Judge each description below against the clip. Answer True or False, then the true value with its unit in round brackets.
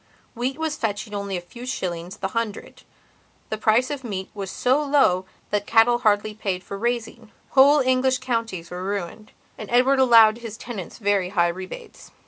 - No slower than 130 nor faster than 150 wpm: False (170 wpm)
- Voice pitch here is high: True (220 Hz)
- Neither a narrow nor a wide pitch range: True (4.2 semitones)